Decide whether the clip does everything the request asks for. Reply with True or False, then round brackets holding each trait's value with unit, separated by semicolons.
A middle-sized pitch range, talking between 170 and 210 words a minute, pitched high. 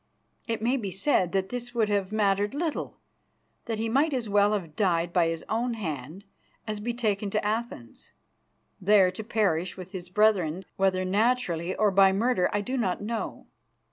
True (3.6 semitones; 175 wpm; 205 Hz)